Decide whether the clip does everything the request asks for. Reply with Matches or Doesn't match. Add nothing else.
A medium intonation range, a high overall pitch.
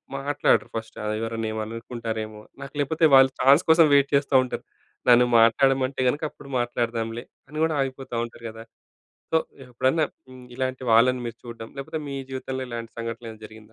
Doesn't match